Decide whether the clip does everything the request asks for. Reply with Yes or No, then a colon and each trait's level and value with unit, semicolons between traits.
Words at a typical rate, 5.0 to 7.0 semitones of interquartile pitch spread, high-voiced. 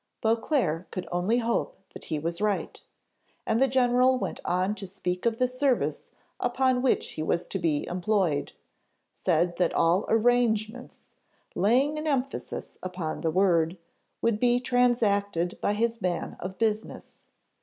Yes: average, 145 wpm; wide, 5.5 semitones; high, 215 Hz